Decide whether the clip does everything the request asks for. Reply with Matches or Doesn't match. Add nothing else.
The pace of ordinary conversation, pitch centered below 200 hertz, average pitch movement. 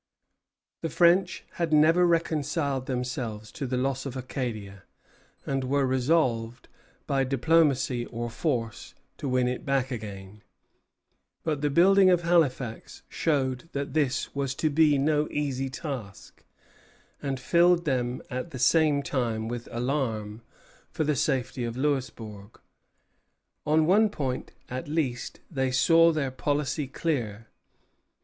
Doesn't match